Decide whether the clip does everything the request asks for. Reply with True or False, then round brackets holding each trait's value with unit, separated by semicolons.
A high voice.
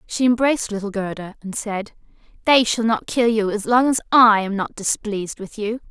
True (220 Hz)